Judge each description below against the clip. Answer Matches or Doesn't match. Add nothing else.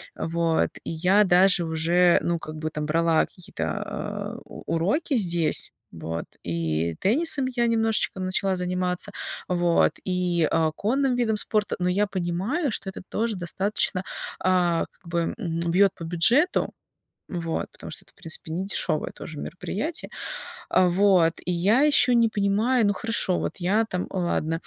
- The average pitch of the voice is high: Doesn't match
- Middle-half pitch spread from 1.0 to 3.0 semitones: Doesn't match